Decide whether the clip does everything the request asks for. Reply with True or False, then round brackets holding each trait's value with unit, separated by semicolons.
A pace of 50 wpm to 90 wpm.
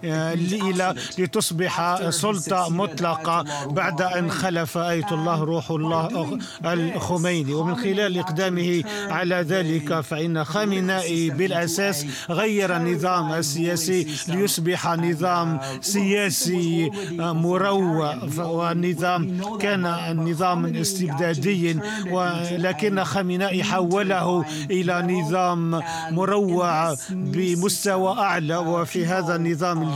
True (80 wpm)